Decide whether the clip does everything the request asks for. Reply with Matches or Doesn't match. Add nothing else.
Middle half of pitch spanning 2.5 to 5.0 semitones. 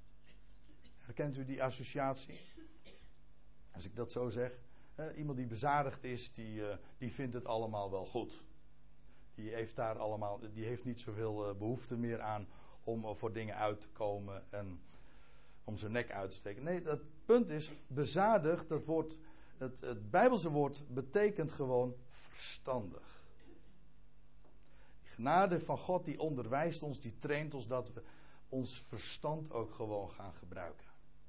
Doesn't match